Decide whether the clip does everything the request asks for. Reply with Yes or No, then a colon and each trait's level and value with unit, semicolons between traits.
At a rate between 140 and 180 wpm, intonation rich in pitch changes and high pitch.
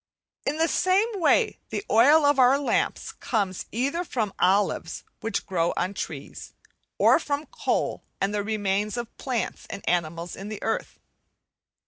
Yes: average, 150 wpm; wide, 6.5 semitones; high, 225 Hz